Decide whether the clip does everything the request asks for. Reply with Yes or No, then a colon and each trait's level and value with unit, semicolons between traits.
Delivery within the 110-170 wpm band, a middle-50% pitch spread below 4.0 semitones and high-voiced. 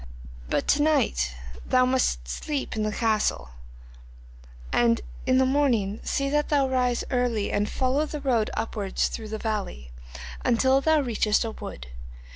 No: average, 155 wpm; average, 4.3 semitones; high, 235 Hz